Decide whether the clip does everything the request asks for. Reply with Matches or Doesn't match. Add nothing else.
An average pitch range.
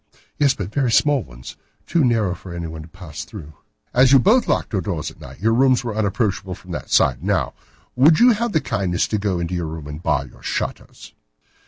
Doesn't match